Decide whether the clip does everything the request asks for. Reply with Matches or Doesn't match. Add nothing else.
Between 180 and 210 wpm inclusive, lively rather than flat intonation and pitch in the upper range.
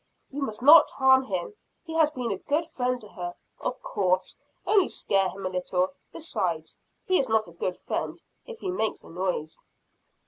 Matches